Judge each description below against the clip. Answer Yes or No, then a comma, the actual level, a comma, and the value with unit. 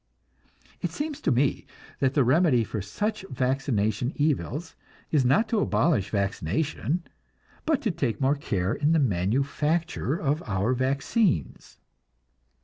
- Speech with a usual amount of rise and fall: No, wide, 5.8 semitones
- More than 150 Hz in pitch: No, low, 135 Hz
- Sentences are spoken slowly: Yes, slow, 130 wpm